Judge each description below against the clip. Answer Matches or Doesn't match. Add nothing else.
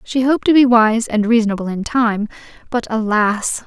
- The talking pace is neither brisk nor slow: Matches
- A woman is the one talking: Matches